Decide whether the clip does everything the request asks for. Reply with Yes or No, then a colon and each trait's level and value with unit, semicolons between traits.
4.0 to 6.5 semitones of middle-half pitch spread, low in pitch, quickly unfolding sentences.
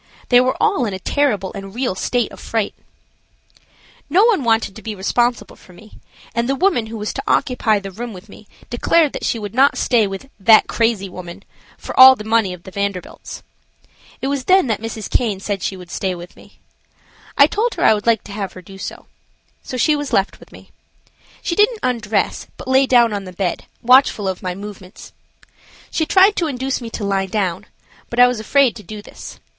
No: average, 4.8 semitones; high, 225 Hz; fast, 210 wpm